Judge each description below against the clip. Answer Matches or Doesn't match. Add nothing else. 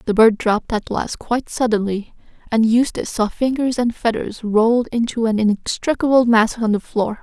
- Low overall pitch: Doesn't match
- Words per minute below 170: Doesn't match